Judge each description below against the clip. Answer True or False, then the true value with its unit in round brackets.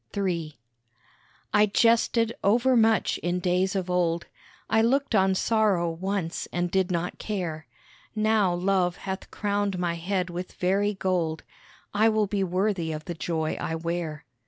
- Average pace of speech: True (150 wpm)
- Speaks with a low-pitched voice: False (185 Hz)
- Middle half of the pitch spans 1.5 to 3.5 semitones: True (3.1 semitones)